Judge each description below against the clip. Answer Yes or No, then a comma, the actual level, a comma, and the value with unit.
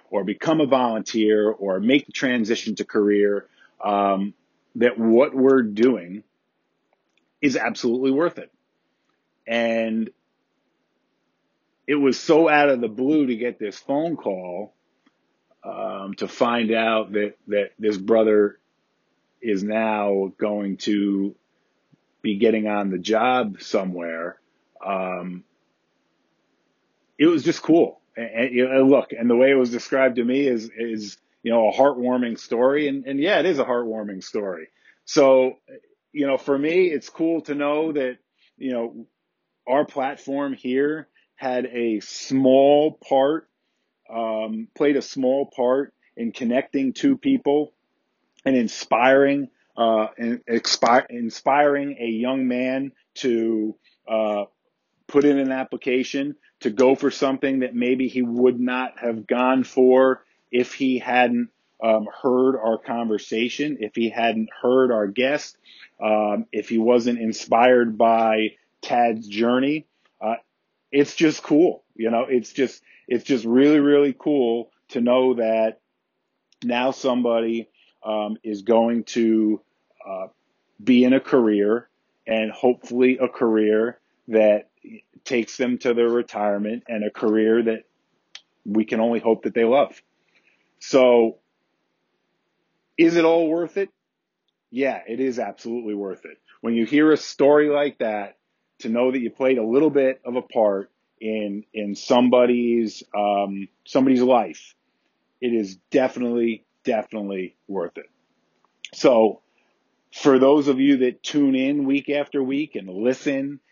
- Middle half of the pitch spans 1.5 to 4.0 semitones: Yes, average, 3.5 semitones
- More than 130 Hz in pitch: No, low, 120 Hz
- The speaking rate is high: No, average, 140 wpm